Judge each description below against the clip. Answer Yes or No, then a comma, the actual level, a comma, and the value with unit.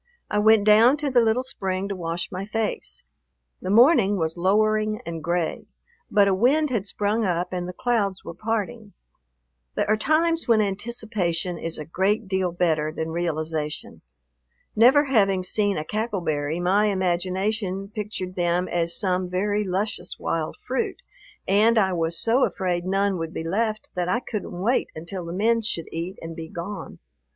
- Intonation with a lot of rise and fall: No, average, 3.7 semitones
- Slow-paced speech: No, average, 170 wpm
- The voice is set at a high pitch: Yes, high, 195 Hz